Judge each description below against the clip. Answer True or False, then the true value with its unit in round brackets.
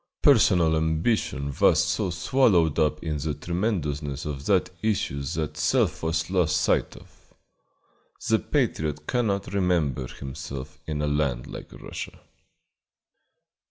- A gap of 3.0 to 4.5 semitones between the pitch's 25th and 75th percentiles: True (3.6 semitones)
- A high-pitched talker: False (80 Hz)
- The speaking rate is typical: False (125 wpm)